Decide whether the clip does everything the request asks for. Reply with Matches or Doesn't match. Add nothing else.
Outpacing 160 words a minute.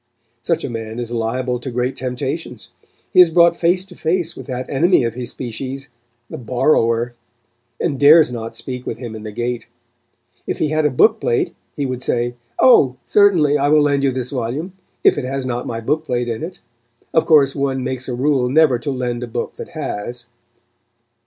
Matches